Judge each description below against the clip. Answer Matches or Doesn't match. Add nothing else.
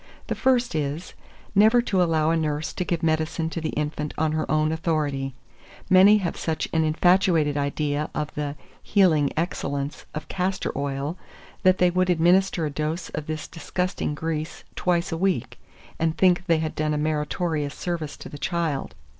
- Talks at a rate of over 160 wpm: Matches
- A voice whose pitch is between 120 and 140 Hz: Doesn't match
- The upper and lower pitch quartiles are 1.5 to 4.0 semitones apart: Matches